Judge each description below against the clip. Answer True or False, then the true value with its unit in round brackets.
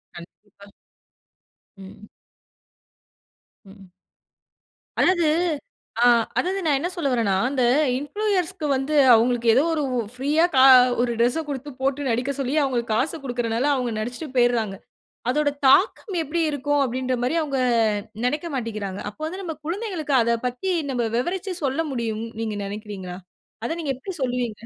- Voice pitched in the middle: False (260 Hz)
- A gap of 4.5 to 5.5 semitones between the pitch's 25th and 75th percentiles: True (4.8 semitones)